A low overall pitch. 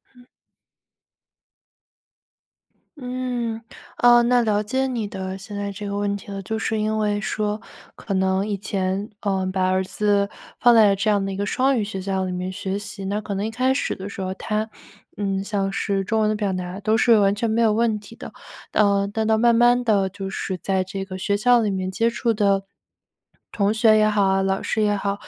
No: high, 205 Hz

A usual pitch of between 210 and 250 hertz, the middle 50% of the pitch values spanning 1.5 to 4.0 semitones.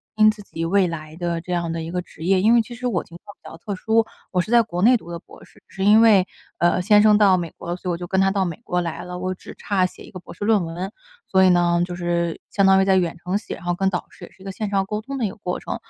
No: medium, 185 Hz; average, 3.0 semitones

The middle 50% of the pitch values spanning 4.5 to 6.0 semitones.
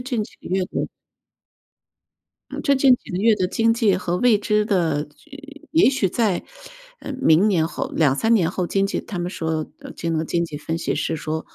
Yes: wide, 5.5 semitones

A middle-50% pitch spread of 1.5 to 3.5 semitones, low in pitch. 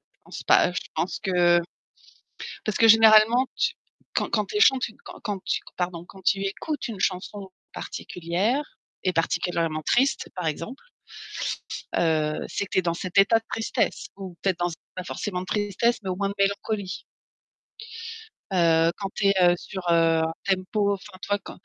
No: average, 3.2 semitones; high, 190 Hz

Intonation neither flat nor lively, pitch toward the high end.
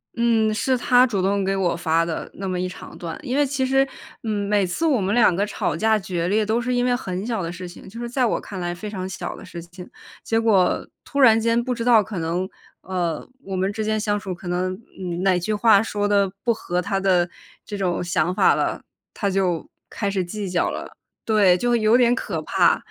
Yes: average, 3.8 semitones; high, 200 Hz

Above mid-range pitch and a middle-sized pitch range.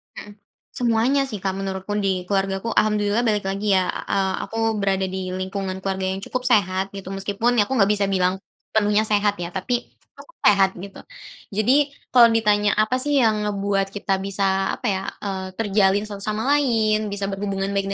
No: high, 200 Hz; narrow, 1.9 semitones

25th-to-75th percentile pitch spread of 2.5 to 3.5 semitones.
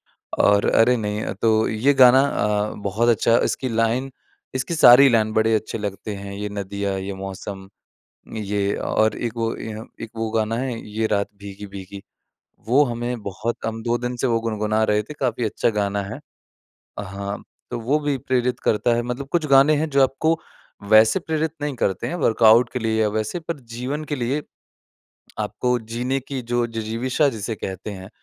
Yes: average, 3.2 semitones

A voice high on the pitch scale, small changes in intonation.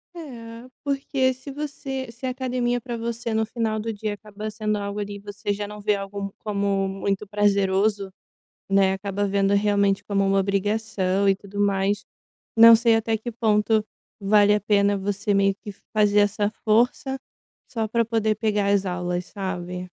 Yes: high, 210 Hz; narrow, 2.3 semitones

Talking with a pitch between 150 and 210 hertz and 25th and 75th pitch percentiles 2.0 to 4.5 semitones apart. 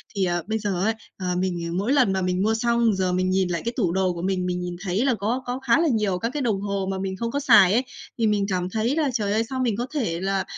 Yes: high, 200 Hz; average, 4.2 semitones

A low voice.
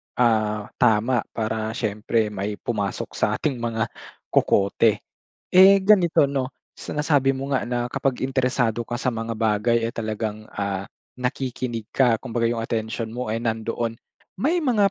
Yes: low, 115 Hz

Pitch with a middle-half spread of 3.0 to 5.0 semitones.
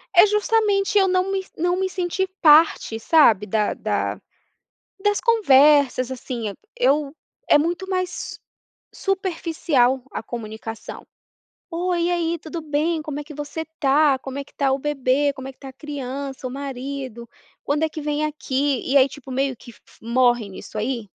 Yes: average, 4.5 semitones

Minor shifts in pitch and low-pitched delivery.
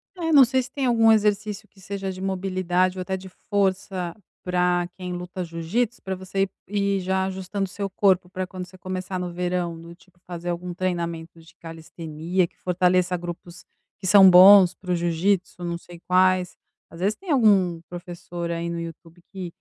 No: narrow, 1.9 semitones; medium, 185 Hz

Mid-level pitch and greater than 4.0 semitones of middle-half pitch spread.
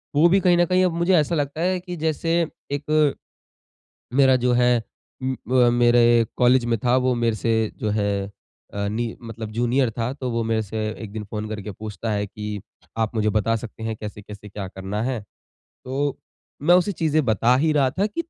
No: low, 120 Hz; average, 5.2 semitones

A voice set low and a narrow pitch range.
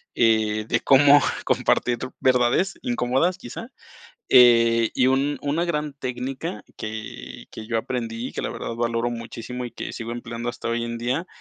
Yes: low, 120 Hz; narrow, 2.2 semitones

